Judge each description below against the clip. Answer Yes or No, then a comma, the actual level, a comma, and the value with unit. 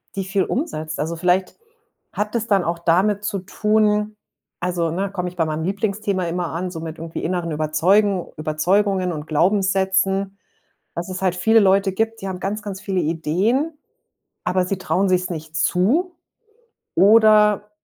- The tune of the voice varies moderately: Yes, average, 3.3 semitones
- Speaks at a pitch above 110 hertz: Yes, high, 190 Hz